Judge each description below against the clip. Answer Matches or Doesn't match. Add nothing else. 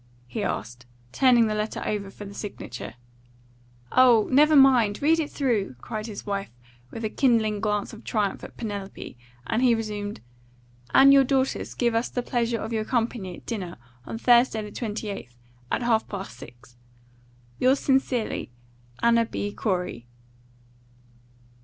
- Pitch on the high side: Matches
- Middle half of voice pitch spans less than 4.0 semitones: Matches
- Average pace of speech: Matches